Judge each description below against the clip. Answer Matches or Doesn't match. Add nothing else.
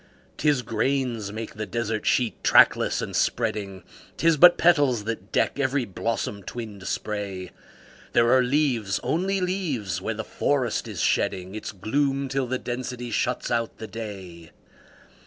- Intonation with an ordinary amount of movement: Matches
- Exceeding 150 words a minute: Doesn't match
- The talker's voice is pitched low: Matches